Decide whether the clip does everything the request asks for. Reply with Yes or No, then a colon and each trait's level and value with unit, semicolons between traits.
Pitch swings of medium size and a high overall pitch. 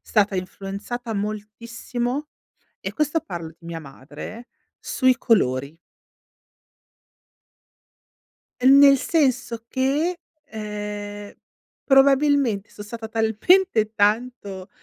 Yes: average, 4.3 semitones; high, 225 Hz